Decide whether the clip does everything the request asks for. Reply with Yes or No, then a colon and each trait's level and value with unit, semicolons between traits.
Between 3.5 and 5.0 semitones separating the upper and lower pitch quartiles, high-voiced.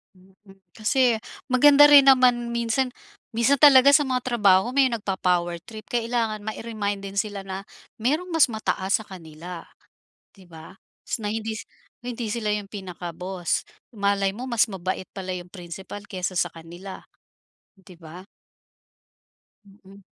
Yes: average, 4.3 semitones; high, 205 Hz